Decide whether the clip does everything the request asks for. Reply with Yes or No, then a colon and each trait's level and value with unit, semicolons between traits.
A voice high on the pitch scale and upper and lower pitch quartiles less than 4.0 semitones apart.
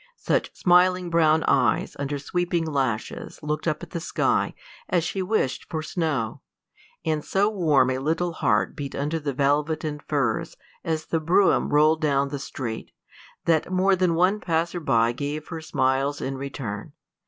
No: medium, 155 Hz; average, 3.4 semitones